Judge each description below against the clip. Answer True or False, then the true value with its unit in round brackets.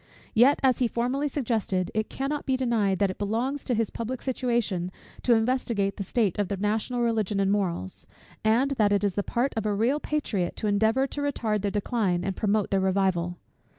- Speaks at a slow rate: False (200 wpm)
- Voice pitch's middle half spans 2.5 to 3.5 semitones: False (3.9 semitones)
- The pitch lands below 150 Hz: False (220 Hz)